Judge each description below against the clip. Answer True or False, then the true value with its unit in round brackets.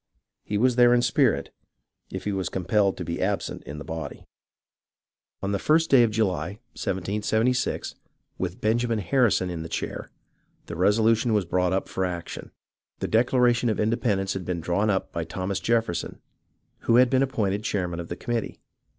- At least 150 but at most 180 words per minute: True (170 wpm)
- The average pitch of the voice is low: True (100 Hz)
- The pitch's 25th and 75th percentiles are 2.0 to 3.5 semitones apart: False (4.4 semitones)